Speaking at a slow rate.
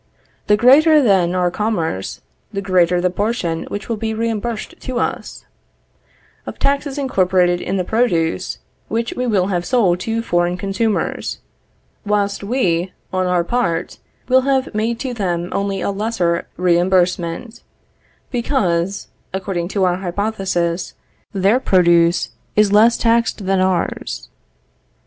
Yes: slow, 130 wpm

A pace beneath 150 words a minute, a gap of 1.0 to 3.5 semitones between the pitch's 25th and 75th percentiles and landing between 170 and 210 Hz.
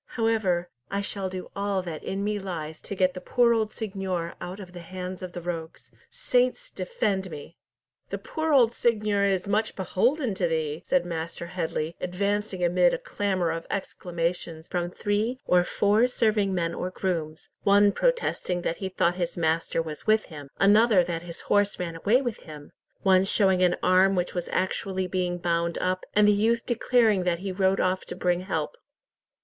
No: average, 185 wpm; average, 3.0 semitones; medium, 185 Hz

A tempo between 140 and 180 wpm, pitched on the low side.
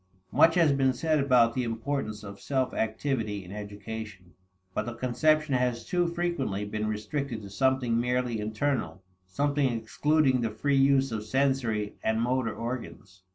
Yes: average, 155 wpm; low, 120 Hz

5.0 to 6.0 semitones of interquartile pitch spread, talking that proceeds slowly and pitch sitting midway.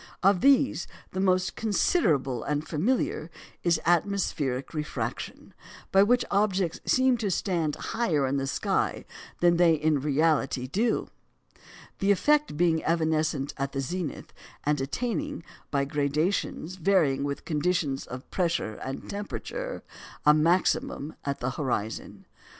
Yes: average, 5.3 semitones; slow, 125 wpm; medium, 160 Hz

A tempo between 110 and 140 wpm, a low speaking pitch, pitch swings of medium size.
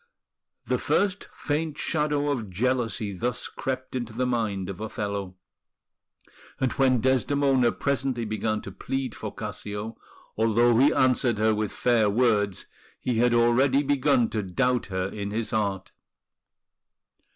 Yes: slow, 135 wpm; low, 120 Hz; average, 3.7 semitones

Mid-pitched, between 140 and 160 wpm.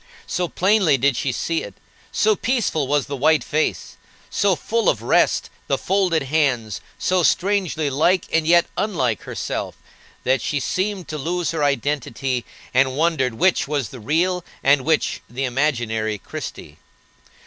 Yes: medium, 150 Hz; average, 150 wpm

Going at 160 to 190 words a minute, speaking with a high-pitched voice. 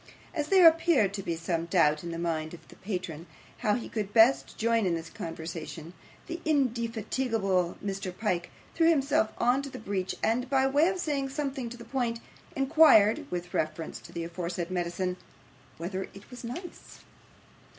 Yes: average, 170 wpm; high, 210 Hz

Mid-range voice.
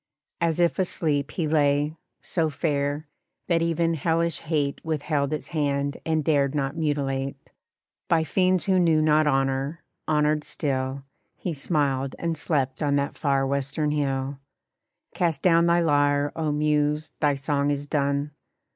Yes: medium, 150 Hz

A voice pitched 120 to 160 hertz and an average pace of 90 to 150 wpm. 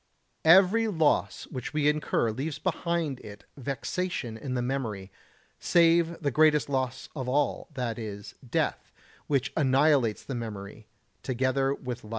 Yes: low, 135 Hz; average, 140 wpm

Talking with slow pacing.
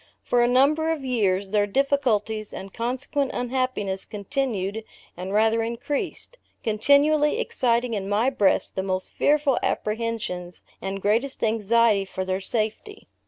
Yes: slow, 130 wpm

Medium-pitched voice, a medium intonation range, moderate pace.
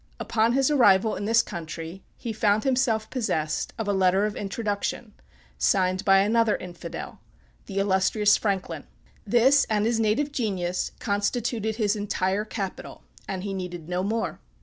No: high, 205 Hz; average, 3.0 semitones; average, 150 wpm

